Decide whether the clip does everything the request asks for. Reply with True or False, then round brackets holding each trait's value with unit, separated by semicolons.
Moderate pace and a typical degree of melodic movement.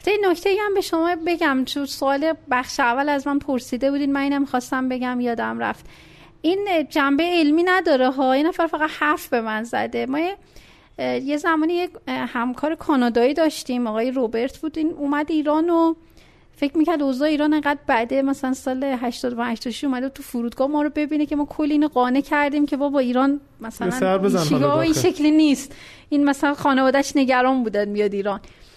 False (175 wpm; 3.5 semitones)